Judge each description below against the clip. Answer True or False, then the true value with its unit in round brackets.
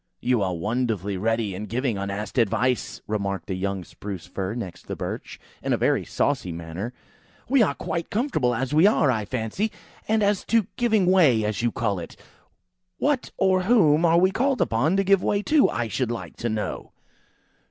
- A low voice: True (120 Hz)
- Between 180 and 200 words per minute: True (185 wpm)